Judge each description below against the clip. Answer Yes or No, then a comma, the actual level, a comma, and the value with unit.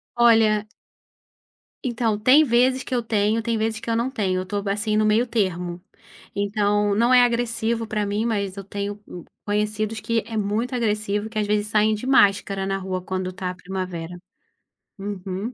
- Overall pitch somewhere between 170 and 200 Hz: No, high, 210 Hz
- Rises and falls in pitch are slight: Yes, narrow, 2.3 semitones